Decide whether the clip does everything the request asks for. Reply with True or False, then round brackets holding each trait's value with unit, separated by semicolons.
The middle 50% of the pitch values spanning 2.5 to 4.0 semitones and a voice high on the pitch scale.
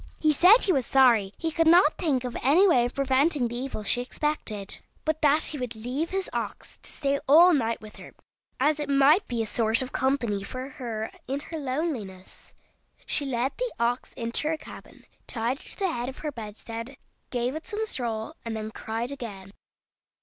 False (4.7 semitones; 260 Hz)